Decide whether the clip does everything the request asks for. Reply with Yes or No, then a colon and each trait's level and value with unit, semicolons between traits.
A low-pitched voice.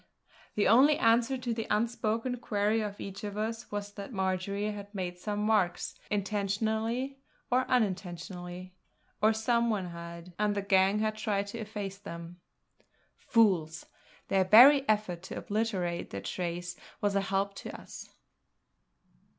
No: high, 205 Hz